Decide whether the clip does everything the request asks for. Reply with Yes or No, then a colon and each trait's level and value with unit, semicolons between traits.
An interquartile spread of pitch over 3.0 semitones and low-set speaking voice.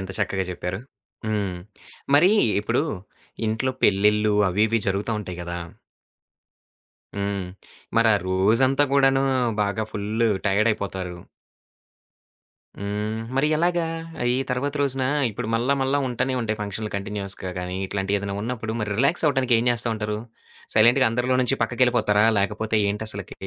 Yes: average, 3.7 semitones; low, 110 Hz